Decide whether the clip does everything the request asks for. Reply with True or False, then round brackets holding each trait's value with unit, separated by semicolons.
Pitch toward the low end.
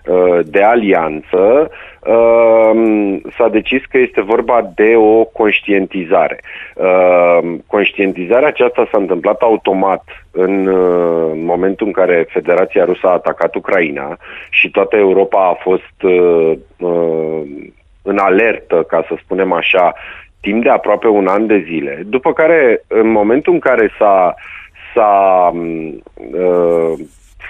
True (90 Hz)